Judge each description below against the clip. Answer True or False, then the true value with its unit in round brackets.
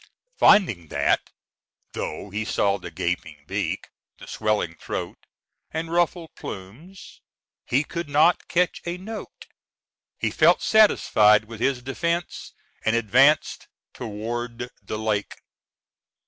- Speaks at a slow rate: True (115 wpm)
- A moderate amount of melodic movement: False (8.2 semitones)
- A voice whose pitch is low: True (120 Hz)